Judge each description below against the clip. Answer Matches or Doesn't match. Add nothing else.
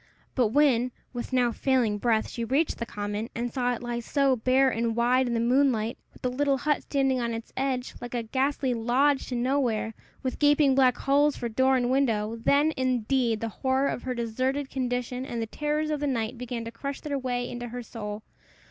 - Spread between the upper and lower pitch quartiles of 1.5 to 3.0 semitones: Matches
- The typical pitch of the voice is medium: Doesn't match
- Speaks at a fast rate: Matches